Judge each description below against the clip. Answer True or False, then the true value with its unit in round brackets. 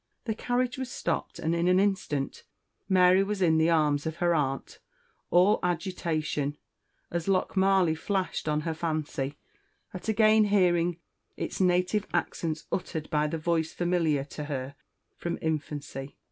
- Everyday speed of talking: True (145 wpm)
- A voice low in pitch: False (170 Hz)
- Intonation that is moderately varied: True (3.5 semitones)